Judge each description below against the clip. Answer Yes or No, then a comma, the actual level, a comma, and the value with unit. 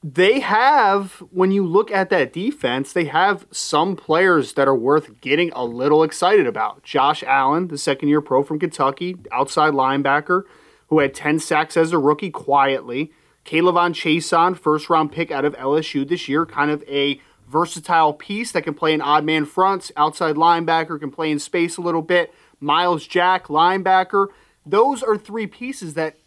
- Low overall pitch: No, medium, 160 Hz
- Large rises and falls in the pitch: No, average, 3.4 semitones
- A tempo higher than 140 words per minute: Yes, average, 180 wpm